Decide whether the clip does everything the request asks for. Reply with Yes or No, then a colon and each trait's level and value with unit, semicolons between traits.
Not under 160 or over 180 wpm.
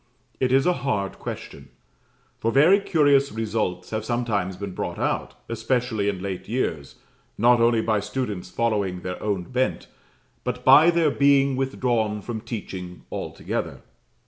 No: average, 145 wpm